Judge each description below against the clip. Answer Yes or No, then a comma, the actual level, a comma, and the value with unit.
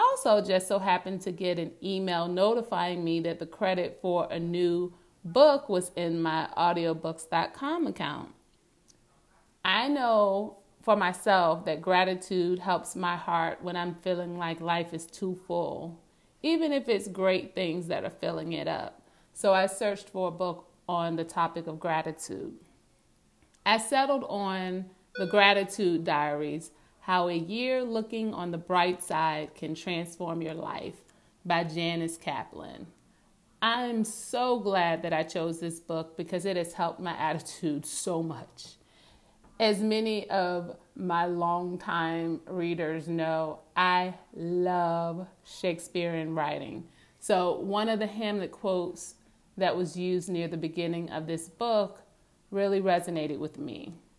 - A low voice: No, medium, 175 Hz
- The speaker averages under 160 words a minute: Yes, average, 140 wpm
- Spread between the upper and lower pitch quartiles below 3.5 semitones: Yes, average, 2.8 semitones